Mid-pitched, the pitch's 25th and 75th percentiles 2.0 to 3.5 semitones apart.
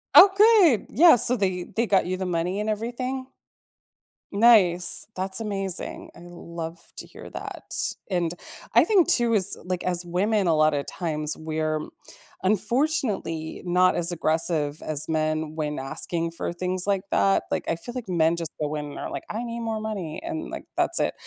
No: medium, 180 Hz; wide, 5.4 semitones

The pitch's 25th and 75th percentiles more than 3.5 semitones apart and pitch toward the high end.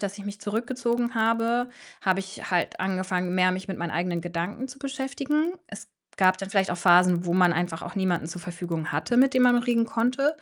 Yes: average, 5.3 semitones; high, 195 Hz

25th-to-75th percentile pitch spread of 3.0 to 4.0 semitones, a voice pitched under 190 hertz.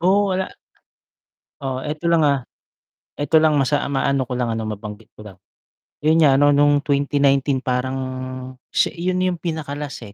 Yes: average, 3.3 semitones; medium, 140 Hz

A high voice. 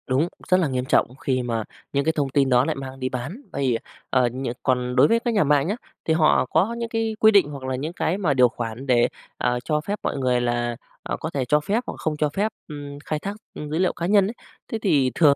No: medium, 145 Hz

